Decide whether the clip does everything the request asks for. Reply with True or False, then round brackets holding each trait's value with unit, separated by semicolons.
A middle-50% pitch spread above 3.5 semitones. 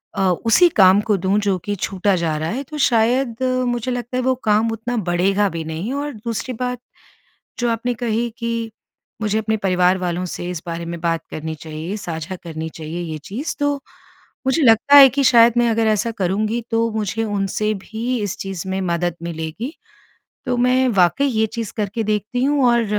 True (4.8 semitones)